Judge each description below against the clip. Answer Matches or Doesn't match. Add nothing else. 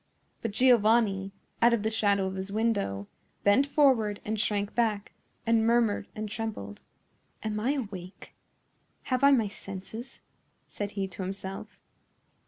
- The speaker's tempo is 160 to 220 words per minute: Doesn't match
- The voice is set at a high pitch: Matches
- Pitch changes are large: Doesn't match